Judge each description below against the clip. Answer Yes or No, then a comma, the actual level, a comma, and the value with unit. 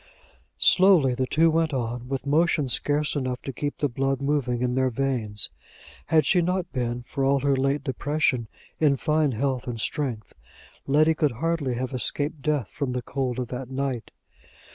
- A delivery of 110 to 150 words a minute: No, average, 175 wpm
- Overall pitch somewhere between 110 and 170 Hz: Yes, low, 135 Hz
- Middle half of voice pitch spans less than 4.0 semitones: Yes, average, 3.1 semitones